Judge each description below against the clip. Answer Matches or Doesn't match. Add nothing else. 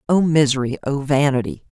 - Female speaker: Matches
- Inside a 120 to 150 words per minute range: Matches